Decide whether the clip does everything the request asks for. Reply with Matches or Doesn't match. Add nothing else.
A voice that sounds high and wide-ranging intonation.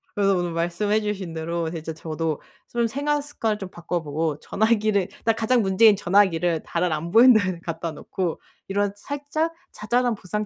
Doesn't match